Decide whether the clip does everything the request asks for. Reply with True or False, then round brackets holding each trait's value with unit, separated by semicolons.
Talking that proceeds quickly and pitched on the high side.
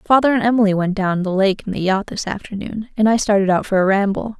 True (260 wpm; 205 Hz)